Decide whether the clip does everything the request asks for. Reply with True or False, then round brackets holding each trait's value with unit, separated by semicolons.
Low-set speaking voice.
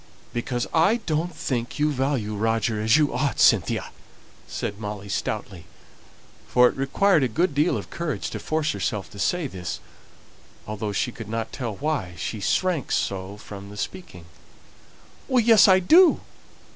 True (125 Hz)